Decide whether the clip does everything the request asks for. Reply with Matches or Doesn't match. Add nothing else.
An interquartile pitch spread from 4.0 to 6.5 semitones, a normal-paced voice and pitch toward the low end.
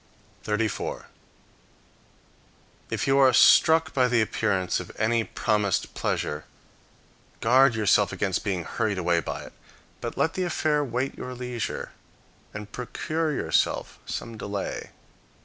Doesn't match